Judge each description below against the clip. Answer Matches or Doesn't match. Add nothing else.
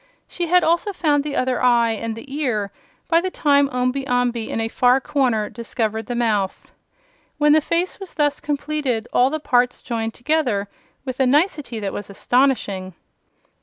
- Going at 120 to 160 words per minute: Doesn't match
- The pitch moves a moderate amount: Matches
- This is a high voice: Matches